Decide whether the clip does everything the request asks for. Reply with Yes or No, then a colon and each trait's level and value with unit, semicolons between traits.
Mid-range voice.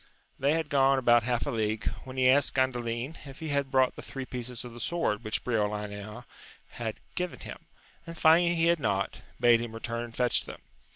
No: low, 125 Hz